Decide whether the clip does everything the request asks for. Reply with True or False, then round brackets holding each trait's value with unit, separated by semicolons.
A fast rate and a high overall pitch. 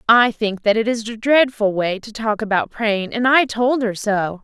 True (215 wpm; 220 Hz)